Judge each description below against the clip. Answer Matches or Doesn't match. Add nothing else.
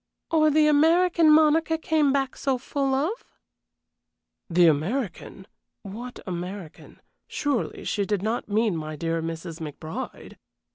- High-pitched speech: Matches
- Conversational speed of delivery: Doesn't match